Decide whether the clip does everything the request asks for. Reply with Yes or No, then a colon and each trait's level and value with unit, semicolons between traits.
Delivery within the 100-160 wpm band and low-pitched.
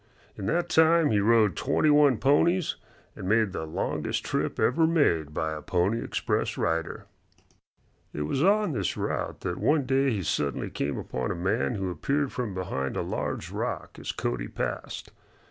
No: average, 175 wpm; low, 115 Hz